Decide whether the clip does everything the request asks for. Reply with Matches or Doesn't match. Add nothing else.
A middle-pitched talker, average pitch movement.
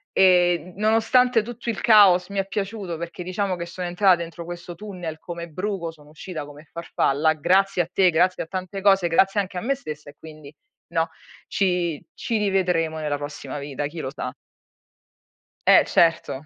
Matches